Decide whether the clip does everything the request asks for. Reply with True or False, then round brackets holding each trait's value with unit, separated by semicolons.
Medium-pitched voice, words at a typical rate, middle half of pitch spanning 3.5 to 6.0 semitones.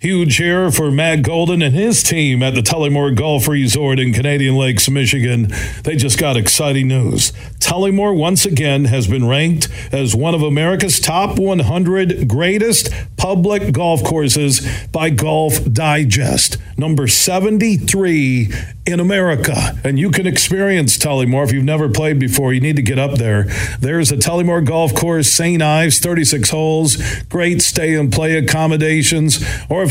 True (145 Hz; 155 wpm; 4.4 semitones)